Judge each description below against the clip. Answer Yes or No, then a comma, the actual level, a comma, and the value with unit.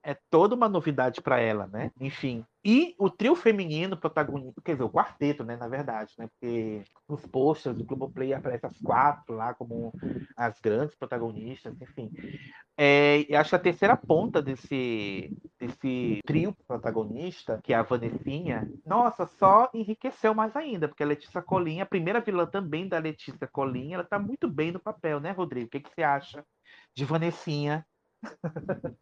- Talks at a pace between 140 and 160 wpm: No, average, 170 wpm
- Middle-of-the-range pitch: Yes, medium, 145 Hz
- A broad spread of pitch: Yes, wide, 6.1 semitones